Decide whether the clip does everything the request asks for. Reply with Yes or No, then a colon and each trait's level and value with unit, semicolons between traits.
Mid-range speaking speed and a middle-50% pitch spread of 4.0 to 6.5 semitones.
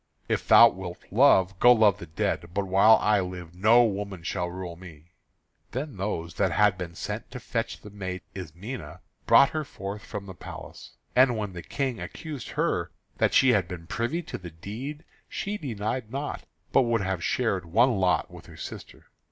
Yes: average, 185 wpm; average, 4.7 semitones